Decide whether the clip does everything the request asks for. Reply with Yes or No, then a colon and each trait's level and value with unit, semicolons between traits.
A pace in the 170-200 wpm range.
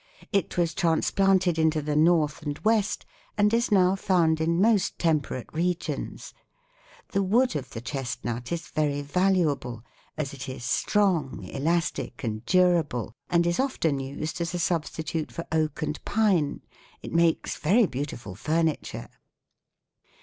No: average, 140 wpm